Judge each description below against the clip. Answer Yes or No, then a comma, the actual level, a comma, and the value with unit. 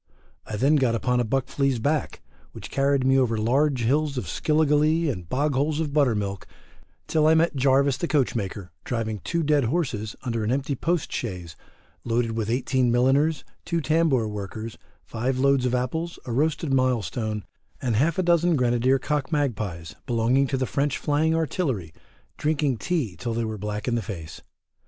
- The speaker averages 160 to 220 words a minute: Yes, average, 175 wpm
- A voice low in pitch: Yes, low, 130 Hz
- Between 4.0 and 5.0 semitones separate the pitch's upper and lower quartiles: Yes, average, 4.6 semitones